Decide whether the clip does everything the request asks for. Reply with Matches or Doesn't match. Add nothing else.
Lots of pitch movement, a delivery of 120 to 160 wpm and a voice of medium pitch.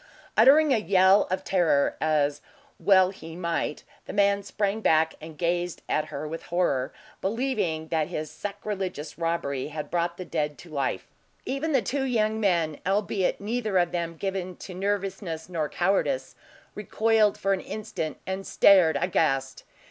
Doesn't match